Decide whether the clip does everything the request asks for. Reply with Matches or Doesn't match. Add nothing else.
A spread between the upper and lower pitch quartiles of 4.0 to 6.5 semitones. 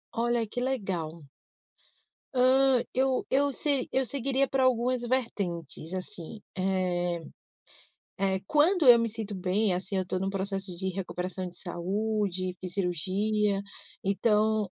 Matches